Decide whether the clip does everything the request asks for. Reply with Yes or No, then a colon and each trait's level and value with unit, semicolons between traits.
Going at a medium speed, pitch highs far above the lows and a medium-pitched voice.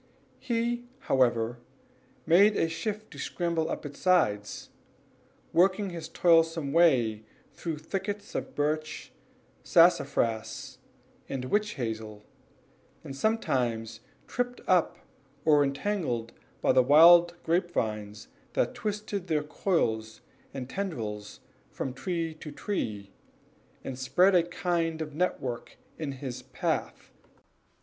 No: slow, 110 wpm; wide, 6.8 semitones; medium, 155 Hz